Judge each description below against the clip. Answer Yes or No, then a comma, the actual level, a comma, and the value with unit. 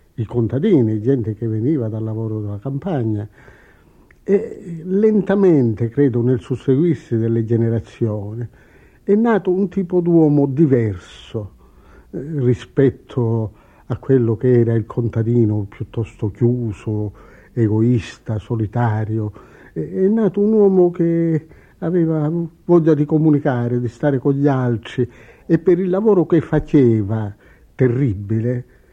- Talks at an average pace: No, slow, 110 wpm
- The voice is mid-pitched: No, low, 125 Hz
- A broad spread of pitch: Yes, wide, 6.1 semitones